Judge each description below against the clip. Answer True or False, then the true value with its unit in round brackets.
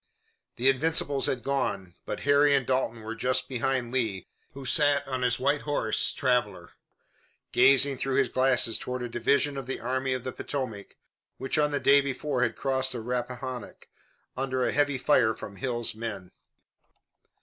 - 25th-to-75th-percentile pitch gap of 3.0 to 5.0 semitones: False (2.4 semitones)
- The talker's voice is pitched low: True (130 Hz)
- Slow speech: False (165 wpm)